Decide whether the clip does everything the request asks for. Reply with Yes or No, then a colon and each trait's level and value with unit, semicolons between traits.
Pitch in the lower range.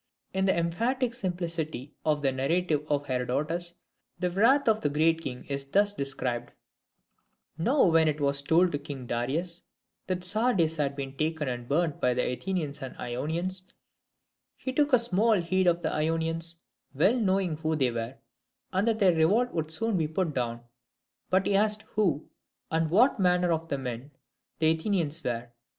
No: medium, 165 Hz